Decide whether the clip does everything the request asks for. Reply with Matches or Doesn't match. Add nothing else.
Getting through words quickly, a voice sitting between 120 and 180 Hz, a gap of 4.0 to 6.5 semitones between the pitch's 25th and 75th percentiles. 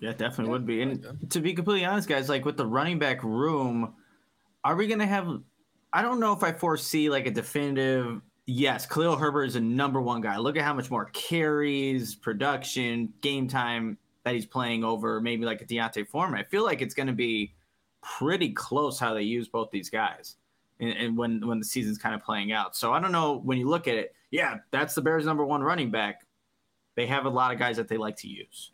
Matches